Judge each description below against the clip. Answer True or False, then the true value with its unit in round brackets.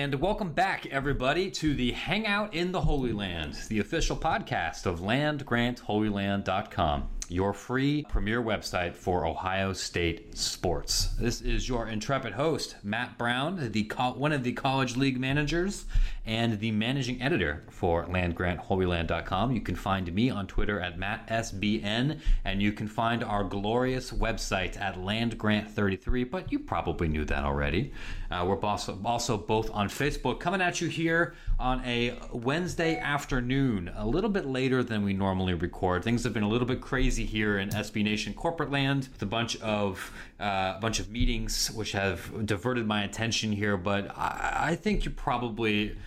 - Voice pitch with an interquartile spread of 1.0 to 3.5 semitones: False (4.5 semitones)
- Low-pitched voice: True (110 Hz)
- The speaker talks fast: False (165 wpm)